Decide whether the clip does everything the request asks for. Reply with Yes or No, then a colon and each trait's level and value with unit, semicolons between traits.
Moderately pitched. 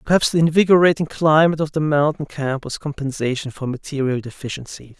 Yes: medium, 145 Hz